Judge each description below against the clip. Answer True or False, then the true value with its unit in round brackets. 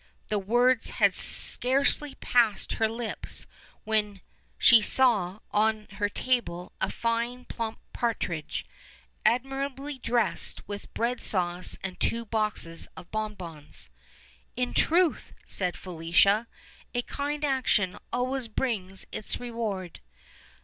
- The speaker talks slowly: True (115 wpm)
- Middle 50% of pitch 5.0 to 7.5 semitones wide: False (4.4 semitones)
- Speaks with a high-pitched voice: True (220 Hz)